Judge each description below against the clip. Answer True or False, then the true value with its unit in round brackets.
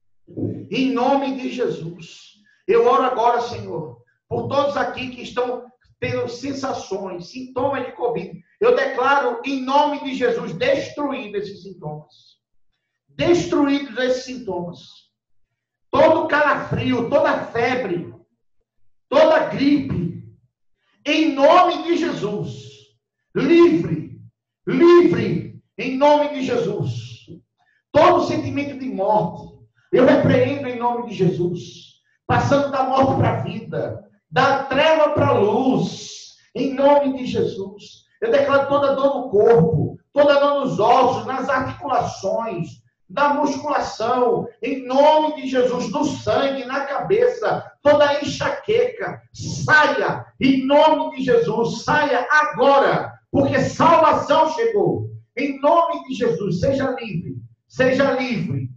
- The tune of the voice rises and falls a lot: True (6.6 semitones)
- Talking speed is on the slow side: True (115 wpm)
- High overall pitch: True (255 Hz)